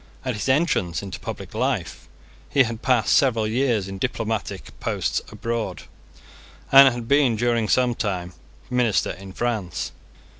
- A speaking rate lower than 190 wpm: Yes, average, 140 wpm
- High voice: No, low, 115 Hz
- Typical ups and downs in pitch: Yes, average, 3.8 semitones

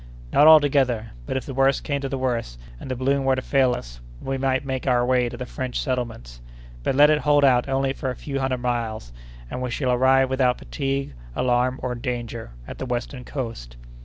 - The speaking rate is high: Yes, fast, 215 wpm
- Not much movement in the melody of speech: Yes, narrow, 1.8 semitones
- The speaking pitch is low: Yes, low, 130 Hz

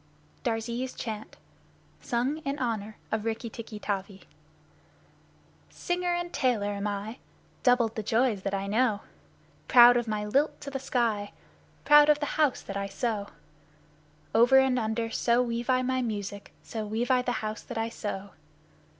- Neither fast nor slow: Yes, average, 160 wpm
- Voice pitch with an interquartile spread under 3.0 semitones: No, average, 3.3 semitones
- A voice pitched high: Yes, high, 230 Hz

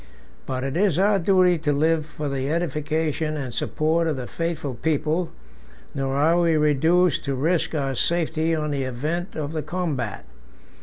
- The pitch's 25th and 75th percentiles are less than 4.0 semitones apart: Yes, average, 3.0 semitones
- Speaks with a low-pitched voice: No, medium, 155 Hz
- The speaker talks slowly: No, average, 165 wpm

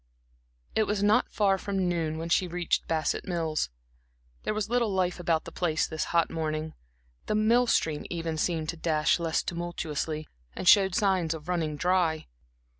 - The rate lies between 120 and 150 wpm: No, average, 170 wpm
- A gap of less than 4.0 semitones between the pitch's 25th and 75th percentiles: Yes, average, 3.2 semitones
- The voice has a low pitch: No, medium, 170 Hz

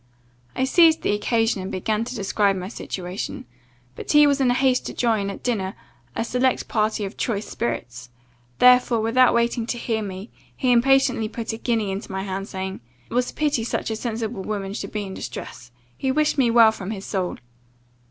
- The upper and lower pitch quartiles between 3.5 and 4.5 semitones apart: Yes, average, 4.1 semitones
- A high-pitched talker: Yes, high, 220 Hz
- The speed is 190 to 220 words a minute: Yes, average, 195 wpm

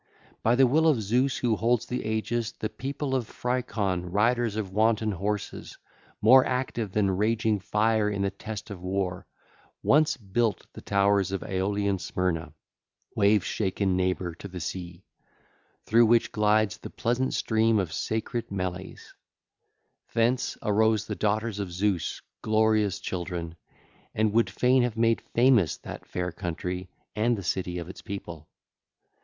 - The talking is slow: No, average, 150 wpm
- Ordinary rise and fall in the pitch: Yes, average, 3.5 semitones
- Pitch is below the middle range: Yes, low, 105 Hz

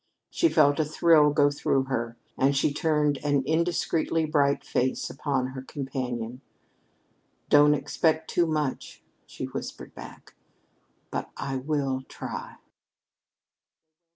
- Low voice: No, medium, 145 Hz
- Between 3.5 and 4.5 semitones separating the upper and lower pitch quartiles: No, average, 2.7 semitones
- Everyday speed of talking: No, slow, 120 wpm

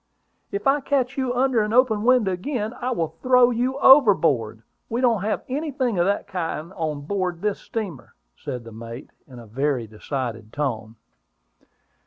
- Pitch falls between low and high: No, high, 200 Hz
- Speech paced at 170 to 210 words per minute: Yes, average, 175 wpm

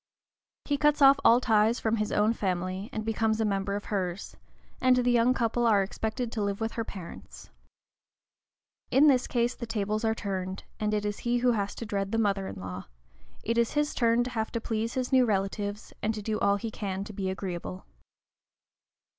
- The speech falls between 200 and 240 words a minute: Yes, fast, 205 wpm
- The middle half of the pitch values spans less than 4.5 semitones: Yes, average, 2.9 semitones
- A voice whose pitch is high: Yes, high, 220 Hz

